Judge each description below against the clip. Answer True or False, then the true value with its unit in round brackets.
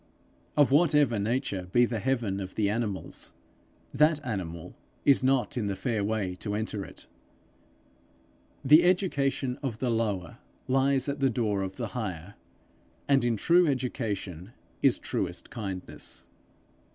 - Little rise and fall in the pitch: False (5.2 semitones)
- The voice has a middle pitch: False (115 Hz)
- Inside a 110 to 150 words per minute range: True (140 wpm)